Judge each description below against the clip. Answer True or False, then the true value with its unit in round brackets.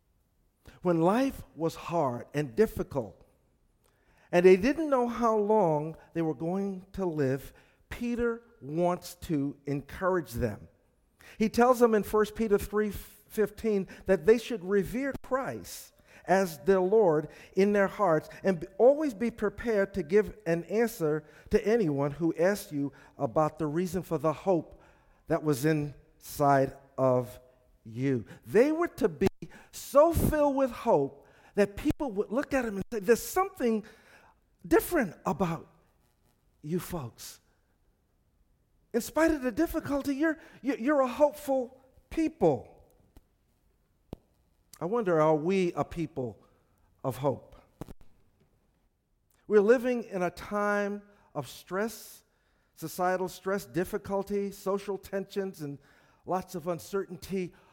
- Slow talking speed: True (125 wpm)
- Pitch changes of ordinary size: False (6.6 semitones)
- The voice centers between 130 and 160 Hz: False (190 Hz)